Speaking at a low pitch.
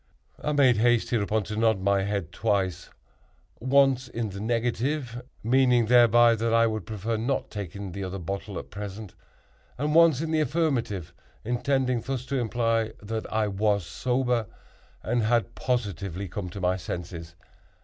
Yes: low, 115 Hz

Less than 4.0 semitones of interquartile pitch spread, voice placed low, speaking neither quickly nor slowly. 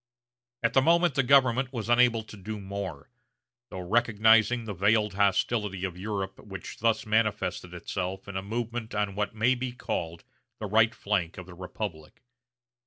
Yes: average, 3.4 semitones; low, 105 Hz; average, 165 wpm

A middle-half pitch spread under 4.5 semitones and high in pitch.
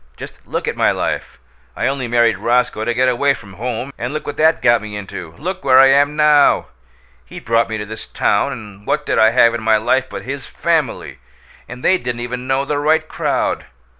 No: average, 4.0 semitones; low, 125 Hz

